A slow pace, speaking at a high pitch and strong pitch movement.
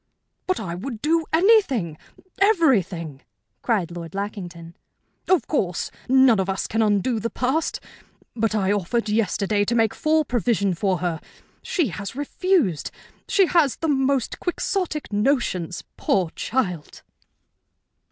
Yes: slow, 130 wpm; high, 225 Hz; wide, 7.4 semitones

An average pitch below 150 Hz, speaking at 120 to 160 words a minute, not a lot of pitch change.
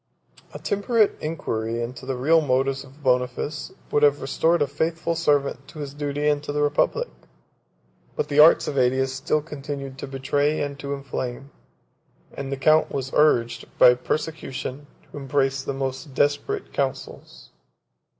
Yes: medium, 140 Hz; average, 155 wpm; narrow, 1.9 semitones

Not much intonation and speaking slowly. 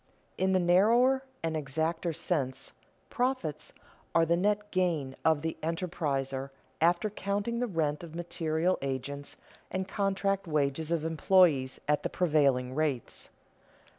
No: average, 4.4 semitones; slow, 130 wpm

